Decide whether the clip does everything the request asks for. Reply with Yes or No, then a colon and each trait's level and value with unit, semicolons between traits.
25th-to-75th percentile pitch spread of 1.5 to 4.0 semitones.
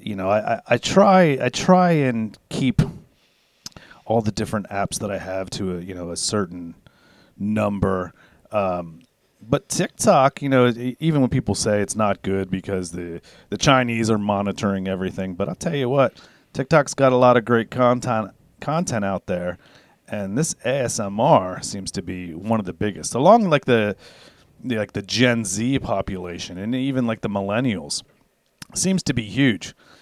No: average, 4.9 semitones